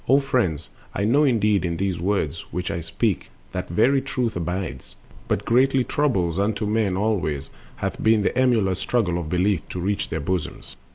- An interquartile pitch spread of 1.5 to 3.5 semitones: No, average, 5.0 semitones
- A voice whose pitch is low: Yes, low, 100 Hz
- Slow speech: No, average, 185 wpm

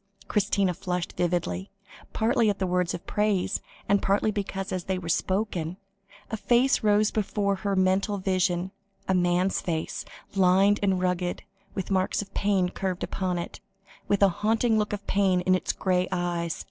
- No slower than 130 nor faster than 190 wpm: Yes, average, 160 wpm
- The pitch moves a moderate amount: No, narrow, 2.1 semitones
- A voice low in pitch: No, high, 190 Hz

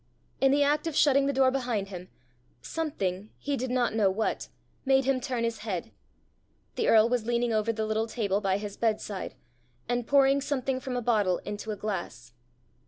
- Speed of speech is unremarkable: Yes, average, 185 wpm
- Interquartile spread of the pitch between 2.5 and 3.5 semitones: No, average, 4.2 semitones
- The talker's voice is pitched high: Yes, high, 230 Hz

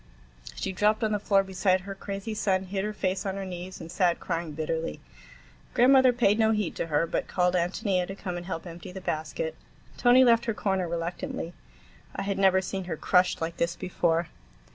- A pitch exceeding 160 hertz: Yes, high, 190 Hz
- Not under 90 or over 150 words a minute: No, average, 200 wpm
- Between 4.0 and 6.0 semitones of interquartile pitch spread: No, average, 3.0 semitones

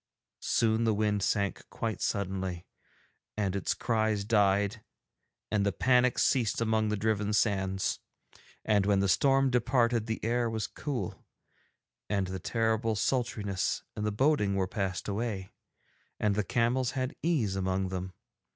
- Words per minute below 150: Yes, average, 140 wpm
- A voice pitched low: Yes, low, 105 Hz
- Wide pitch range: No, average, 3.0 semitones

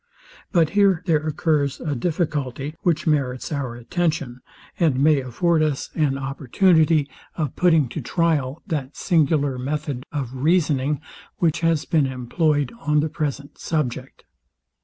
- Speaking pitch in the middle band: Yes, medium, 150 Hz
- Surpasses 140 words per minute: No, slow, 135 wpm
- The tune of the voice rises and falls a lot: No, average, 3.2 semitones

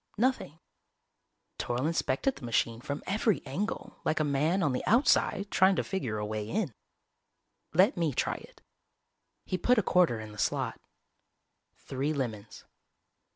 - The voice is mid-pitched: Yes, medium, 150 Hz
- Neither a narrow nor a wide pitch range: No, wide, 8.0 semitones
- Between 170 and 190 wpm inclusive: No, average, 150 wpm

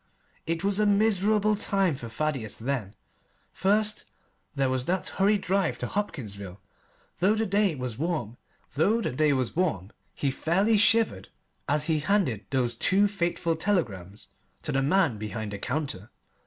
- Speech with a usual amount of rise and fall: No, wide, 8.6 semitones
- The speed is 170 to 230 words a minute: No, slow, 135 wpm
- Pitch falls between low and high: Yes, medium, 155 Hz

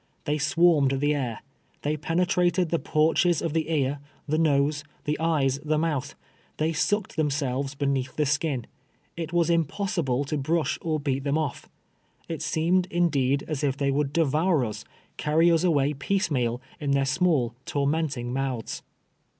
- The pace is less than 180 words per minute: Yes, average, 160 wpm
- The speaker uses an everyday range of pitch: Yes, average, 3.1 semitones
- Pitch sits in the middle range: Yes, medium, 150 Hz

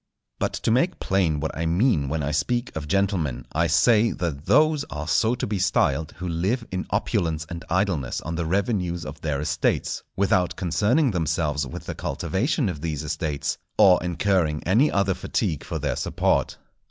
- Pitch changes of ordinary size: Yes, average, 4.6 semitones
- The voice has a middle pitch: No, very low, 90 Hz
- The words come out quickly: No, average, 175 wpm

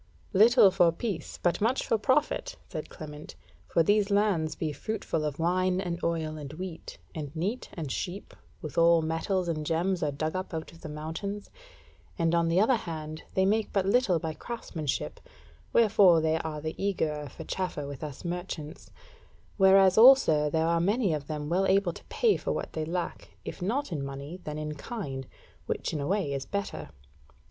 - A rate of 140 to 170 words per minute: No, average, 185 wpm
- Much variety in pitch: No, average, 4.1 semitones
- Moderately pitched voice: Yes, medium, 170 Hz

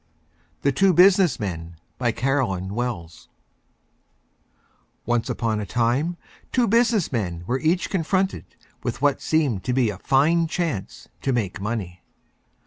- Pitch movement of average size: No, wide, 8.1 semitones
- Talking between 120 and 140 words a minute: Yes, slow, 135 wpm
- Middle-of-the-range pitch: No, low, 125 Hz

